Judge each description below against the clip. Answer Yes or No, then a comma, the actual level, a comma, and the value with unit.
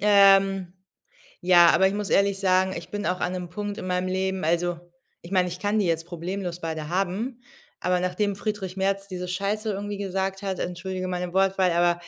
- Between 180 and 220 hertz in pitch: Yes, high, 190 Hz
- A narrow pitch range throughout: Yes, narrow, 1.7 semitones